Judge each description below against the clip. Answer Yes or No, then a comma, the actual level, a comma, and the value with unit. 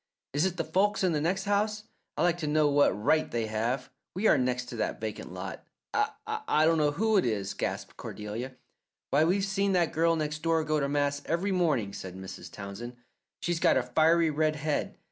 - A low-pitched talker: No, medium, 155 Hz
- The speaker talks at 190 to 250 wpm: Yes, average, 200 wpm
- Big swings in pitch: Yes, wide, 5.7 semitones